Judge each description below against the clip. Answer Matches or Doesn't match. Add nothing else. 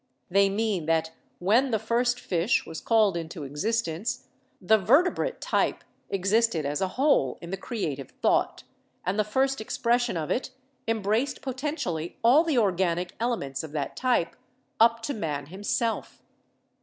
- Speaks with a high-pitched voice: Matches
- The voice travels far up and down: Matches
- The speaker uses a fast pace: Doesn't match